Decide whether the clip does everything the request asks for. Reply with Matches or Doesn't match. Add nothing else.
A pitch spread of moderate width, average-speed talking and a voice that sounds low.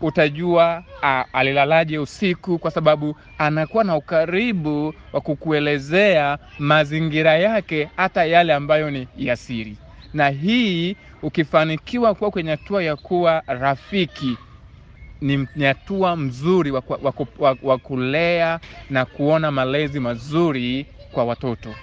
Doesn't match